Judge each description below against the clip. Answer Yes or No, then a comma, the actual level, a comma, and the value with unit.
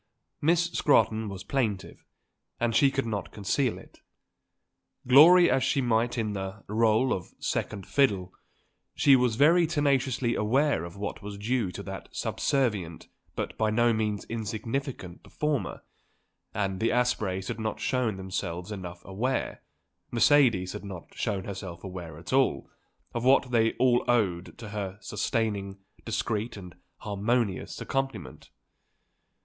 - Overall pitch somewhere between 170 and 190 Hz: No, low, 110 Hz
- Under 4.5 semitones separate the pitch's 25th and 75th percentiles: No, average, 4.8 semitones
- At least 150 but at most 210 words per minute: No, slow, 135 wpm